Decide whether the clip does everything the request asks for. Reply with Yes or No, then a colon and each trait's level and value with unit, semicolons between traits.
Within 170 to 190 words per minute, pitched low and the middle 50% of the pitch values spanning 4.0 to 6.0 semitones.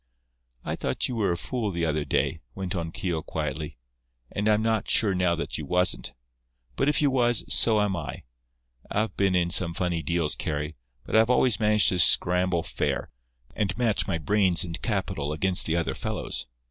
Yes: average, 185 wpm; very low, 90 Hz; average, 4.3 semitones